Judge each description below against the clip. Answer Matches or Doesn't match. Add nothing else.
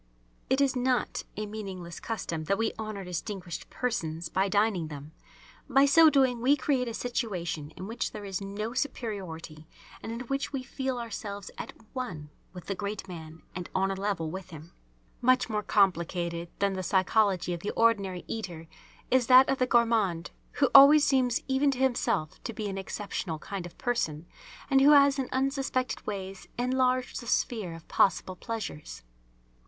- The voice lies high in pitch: Matches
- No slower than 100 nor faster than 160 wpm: Doesn't match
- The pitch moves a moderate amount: Doesn't match